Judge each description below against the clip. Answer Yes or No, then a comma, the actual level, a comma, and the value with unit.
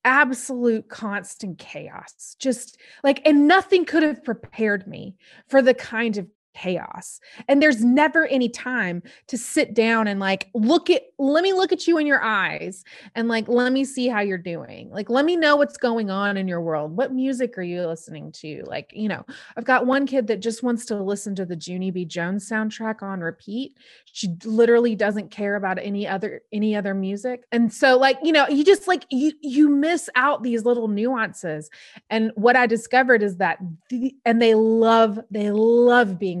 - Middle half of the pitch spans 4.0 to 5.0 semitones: Yes, average, 4.7 semitones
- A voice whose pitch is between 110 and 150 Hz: No, high, 230 Hz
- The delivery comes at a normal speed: Yes, average, 195 wpm